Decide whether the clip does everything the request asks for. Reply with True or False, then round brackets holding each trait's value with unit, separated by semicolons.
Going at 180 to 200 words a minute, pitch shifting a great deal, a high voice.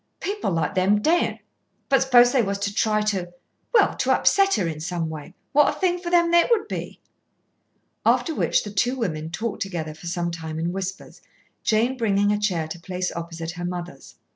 True (195 wpm; 6.3 semitones; 195 Hz)